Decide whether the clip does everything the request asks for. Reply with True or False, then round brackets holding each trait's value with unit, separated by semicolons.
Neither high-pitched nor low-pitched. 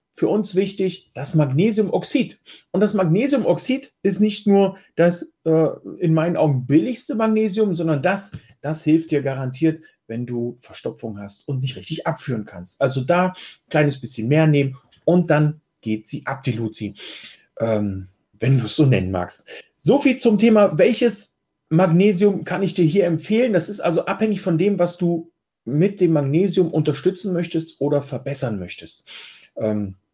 True (160 Hz)